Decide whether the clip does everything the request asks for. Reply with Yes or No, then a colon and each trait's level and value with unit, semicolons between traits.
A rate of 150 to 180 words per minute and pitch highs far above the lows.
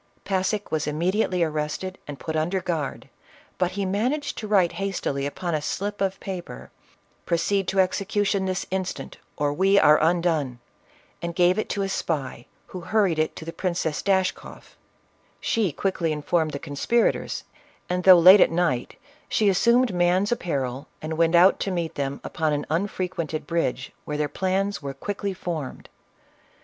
No: average, 165 wpm; average, 3.8 semitones